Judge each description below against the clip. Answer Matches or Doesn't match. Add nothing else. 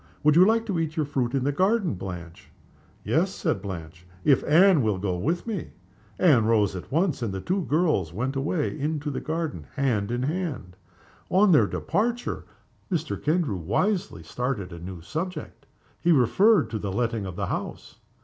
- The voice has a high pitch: Doesn't match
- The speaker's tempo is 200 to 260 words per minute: Doesn't match